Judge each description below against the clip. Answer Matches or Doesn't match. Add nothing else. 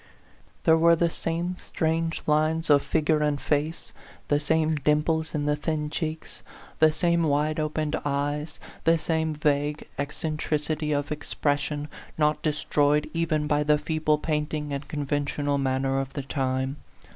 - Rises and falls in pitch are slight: Matches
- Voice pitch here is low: Doesn't match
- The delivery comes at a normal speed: Matches